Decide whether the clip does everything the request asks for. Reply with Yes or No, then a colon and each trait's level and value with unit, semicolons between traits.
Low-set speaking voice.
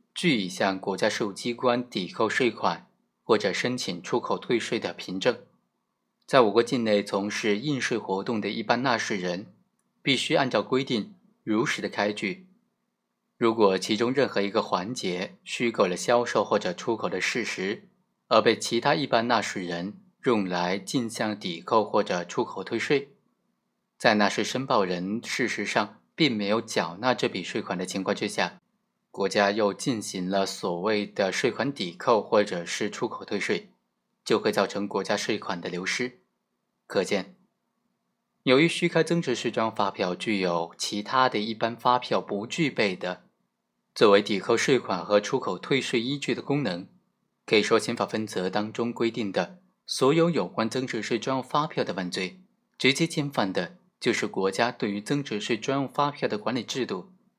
Yes: low, 115 Hz